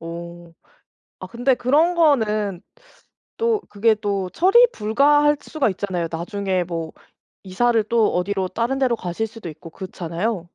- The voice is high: Yes, high, 210 Hz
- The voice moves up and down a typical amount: No, wide, 5.8 semitones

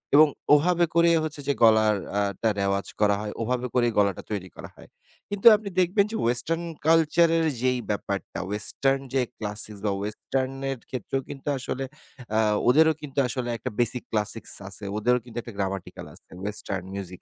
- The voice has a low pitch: Yes, low, 125 Hz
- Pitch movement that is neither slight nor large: No, wide, 5.9 semitones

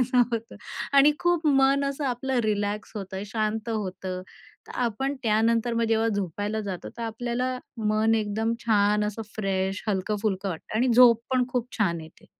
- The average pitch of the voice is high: Yes, high, 220 Hz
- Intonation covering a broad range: No, average, 3.2 semitones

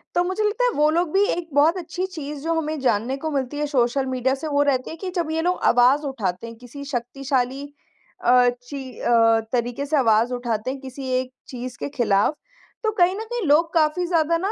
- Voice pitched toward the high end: Yes, very high, 280 Hz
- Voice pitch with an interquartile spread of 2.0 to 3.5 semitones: No, average, 5.0 semitones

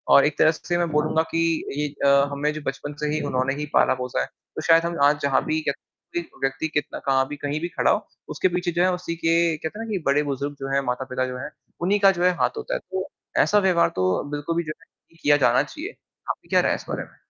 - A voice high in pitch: No, medium, 150 Hz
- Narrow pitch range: No, average, 3.6 semitones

